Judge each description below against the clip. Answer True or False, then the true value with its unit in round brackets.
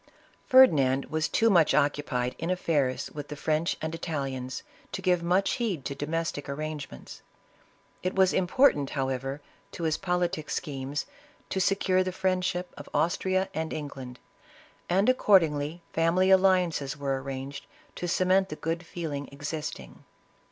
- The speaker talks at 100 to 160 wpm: True (145 wpm)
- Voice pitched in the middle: True (160 Hz)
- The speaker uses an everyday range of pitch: True (4.5 semitones)